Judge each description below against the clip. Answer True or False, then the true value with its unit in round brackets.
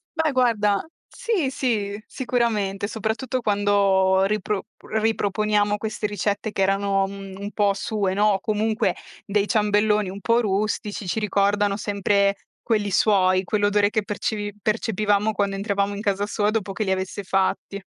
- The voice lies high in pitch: True (205 Hz)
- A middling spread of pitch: False (1.4 semitones)